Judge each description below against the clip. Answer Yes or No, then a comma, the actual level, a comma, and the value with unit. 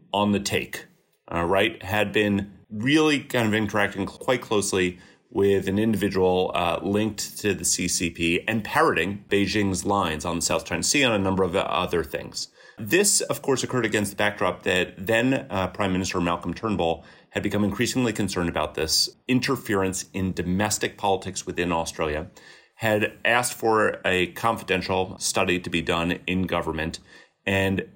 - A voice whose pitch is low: Yes, low, 100 Hz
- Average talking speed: Yes, average, 160 wpm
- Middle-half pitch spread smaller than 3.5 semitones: Yes, average, 3.0 semitones